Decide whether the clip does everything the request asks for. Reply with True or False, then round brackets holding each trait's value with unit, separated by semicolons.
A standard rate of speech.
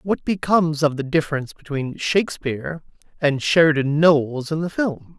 True (150 wpm)